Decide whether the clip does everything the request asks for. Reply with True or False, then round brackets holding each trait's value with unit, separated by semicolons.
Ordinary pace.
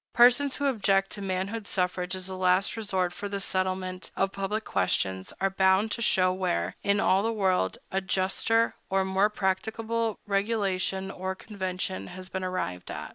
True (170 wpm)